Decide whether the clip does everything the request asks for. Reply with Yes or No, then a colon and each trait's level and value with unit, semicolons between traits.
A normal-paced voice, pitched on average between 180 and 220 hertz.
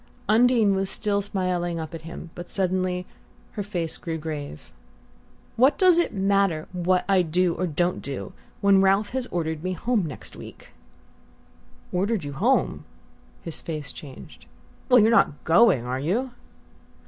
Yes: average, 150 wpm; medium, 185 Hz